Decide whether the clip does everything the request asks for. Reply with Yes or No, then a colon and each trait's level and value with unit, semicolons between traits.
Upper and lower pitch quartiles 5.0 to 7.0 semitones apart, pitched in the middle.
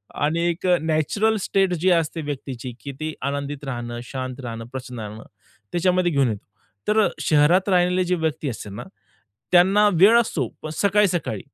Yes: wide, 5.6 semitones; medium, 155 Hz